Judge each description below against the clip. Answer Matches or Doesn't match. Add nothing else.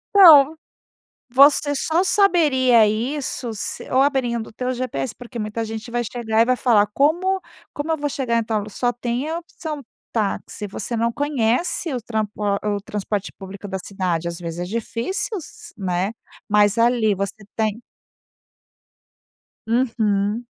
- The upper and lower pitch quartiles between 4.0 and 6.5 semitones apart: Matches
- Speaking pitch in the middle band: Doesn't match